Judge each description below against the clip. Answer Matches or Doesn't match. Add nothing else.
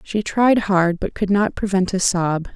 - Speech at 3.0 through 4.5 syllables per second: Matches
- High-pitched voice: Matches